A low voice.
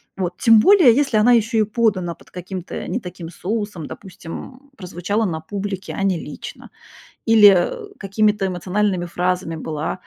No: high, 195 Hz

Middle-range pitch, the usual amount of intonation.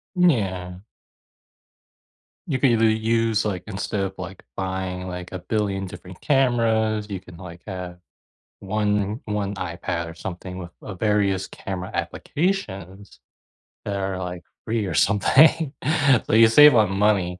No: low, 100 Hz; average, 3.2 semitones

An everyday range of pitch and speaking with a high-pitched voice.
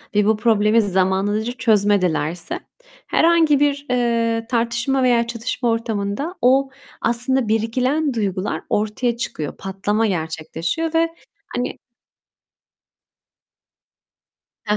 Yes: average, 3.8 semitones; high, 230 Hz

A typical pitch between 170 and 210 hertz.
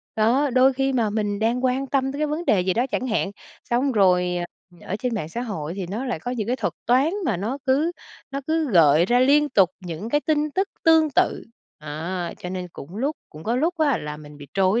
No: high, 235 Hz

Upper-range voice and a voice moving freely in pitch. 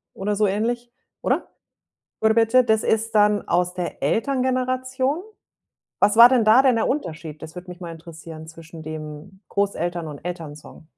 Yes: high, 200 Hz; wide, 6.1 semitones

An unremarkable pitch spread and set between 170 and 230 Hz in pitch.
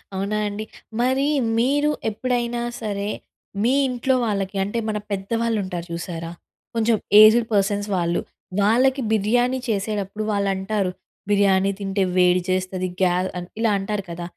Yes: average, 3.3 semitones; high, 205 Hz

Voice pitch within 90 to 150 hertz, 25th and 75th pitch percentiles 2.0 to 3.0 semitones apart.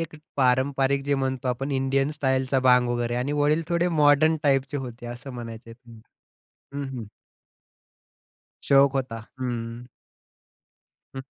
Yes: low, 135 Hz; narrow, 2.4 semitones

